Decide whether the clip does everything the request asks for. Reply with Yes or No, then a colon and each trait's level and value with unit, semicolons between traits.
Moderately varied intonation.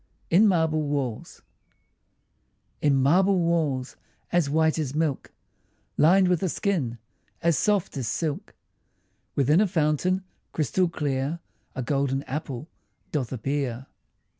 Yes: average, 3.9 semitones